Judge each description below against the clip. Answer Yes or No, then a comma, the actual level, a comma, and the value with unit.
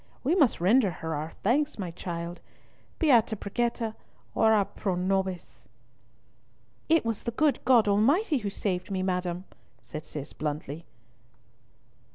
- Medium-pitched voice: No, high, 200 Hz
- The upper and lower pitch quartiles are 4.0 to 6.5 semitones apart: Yes, average, 5.2 semitones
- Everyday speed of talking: No, slow, 130 wpm